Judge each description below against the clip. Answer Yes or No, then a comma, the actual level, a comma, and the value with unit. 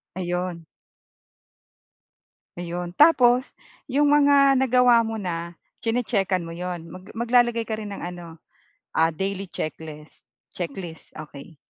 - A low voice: No, medium, 185 Hz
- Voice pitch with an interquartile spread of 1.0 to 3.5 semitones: No, wide, 6.0 semitones